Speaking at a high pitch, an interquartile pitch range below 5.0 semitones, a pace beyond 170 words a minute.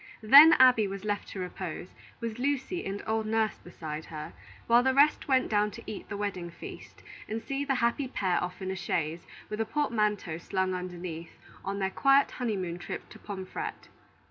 No: high, 205 Hz; average, 5.3 semitones; average, 190 wpm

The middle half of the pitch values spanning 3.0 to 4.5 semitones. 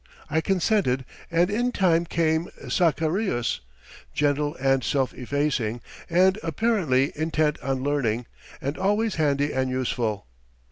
No: average, 4.9 semitones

